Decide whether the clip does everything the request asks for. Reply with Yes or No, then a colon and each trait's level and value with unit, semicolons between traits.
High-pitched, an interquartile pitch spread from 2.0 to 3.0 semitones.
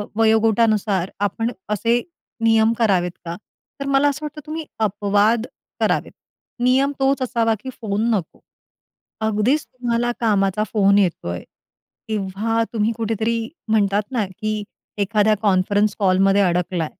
Yes: high, 215 Hz; narrow, 2.6 semitones